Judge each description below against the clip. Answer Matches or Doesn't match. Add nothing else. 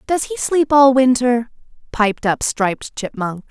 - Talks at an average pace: Matches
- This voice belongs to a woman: Matches